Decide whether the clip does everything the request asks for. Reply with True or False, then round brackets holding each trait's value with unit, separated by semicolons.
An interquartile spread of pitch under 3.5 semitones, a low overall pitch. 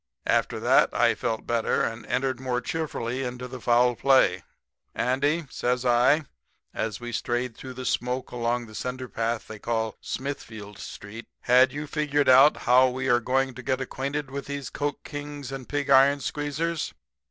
True (2.7 semitones; 130 Hz)